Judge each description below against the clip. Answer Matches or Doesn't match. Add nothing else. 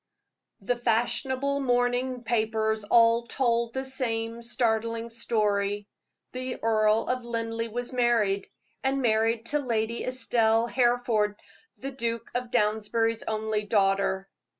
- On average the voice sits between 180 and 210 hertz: Doesn't match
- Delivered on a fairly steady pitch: Matches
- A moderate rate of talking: Doesn't match